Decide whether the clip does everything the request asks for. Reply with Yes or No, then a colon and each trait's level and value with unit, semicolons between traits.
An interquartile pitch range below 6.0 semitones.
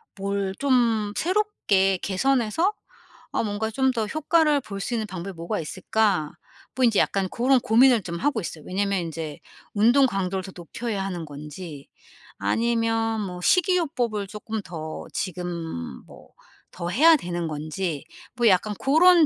Yes: wide, 5.5 semitones